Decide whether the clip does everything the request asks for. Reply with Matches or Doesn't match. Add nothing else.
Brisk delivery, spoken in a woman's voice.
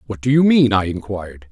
Doesn't match